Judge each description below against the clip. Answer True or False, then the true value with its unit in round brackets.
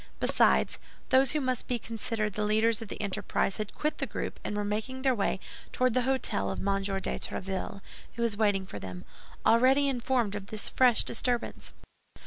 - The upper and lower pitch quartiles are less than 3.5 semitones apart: False (3.8 semitones)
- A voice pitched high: True (220 Hz)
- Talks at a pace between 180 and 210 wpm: True (185 wpm)